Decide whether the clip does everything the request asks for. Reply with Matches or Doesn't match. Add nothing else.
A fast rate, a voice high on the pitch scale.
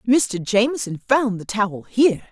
Doesn't match